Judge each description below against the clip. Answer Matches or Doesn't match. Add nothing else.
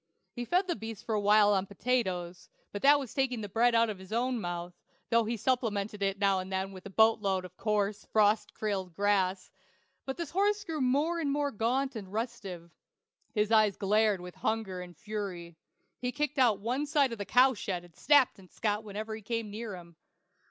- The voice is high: Matches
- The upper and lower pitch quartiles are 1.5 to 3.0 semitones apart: Doesn't match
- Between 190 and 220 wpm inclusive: Matches